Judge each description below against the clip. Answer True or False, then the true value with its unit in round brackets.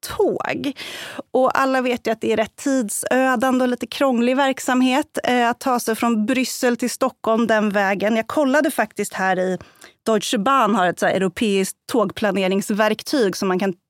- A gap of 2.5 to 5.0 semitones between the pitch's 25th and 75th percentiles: True (3.9 semitones)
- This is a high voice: True (235 Hz)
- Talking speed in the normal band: True (170 wpm)